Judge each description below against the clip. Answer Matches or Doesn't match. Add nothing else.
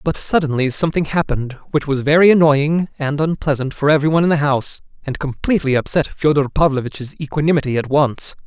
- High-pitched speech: Doesn't match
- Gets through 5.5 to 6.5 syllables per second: Matches